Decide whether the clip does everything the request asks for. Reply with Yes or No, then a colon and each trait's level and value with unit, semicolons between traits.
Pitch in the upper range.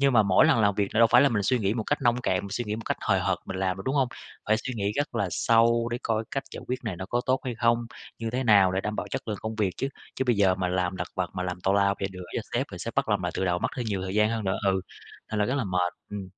No: low, 105 Hz